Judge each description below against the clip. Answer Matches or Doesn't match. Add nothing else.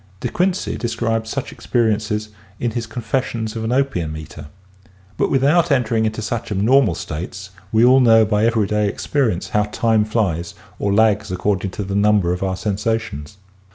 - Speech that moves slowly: Doesn't match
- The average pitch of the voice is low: Matches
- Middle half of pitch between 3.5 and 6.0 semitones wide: Doesn't match